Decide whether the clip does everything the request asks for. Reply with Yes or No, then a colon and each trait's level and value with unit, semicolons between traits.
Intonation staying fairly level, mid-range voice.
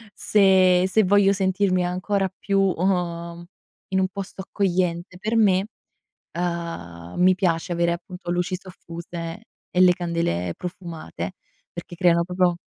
Yes: narrow, 1.9 semitones; medium, 180 Hz